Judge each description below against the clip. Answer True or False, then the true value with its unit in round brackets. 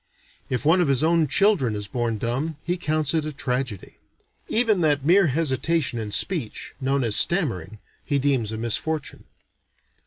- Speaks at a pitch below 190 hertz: True (140 Hz)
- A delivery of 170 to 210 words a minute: False (160 wpm)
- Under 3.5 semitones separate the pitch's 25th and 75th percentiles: False (5.5 semitones)